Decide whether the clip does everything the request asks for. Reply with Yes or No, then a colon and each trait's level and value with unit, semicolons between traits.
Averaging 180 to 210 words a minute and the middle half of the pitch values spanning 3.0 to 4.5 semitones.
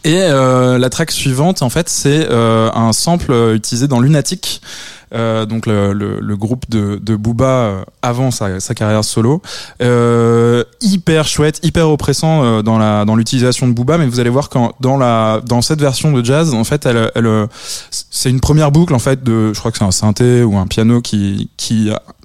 Yes: average, 200 wpm; average, 4.0 semitones